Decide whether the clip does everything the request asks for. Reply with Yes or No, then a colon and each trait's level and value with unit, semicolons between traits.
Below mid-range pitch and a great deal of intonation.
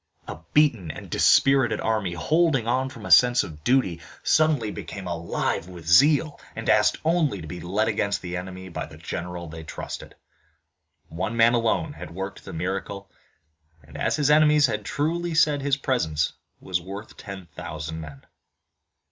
Yes: low, 105 Hz; wide, 7.7 semitones